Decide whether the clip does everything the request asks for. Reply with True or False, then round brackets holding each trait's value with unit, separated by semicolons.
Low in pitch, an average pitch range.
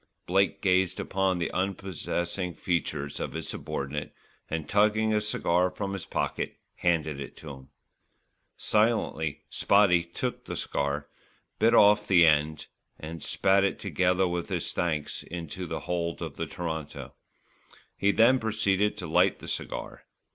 True (90 Hz; 3.8 semitones)